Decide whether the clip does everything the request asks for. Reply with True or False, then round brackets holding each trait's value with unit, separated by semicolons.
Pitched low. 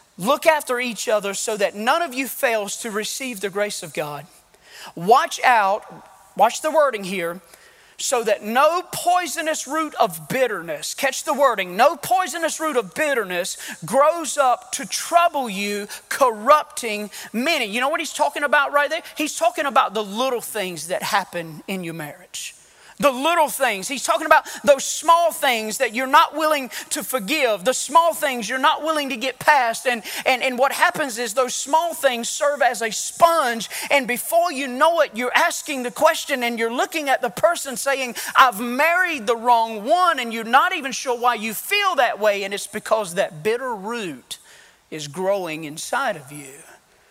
False (260 Hz)